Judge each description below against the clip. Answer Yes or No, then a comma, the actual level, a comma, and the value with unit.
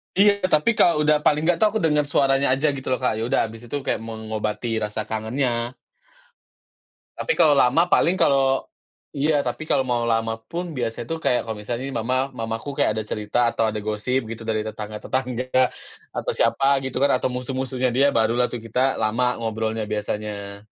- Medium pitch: No, low, 125 Hz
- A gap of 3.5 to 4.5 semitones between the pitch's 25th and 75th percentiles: Yes, average, 4.0 semitones